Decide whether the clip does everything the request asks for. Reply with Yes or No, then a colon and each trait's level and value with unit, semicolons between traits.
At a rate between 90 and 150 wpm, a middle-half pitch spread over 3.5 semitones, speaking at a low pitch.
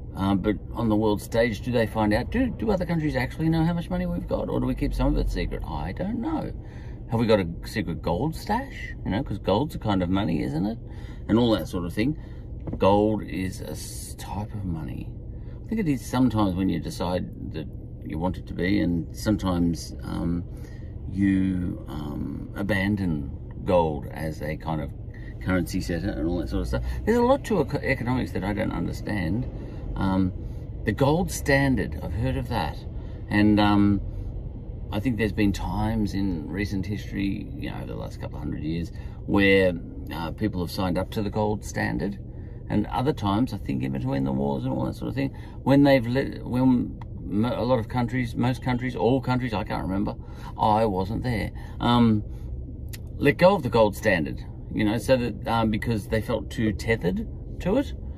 No: average, 195 wpm; average, 4.0 semitones; low, 105 Hz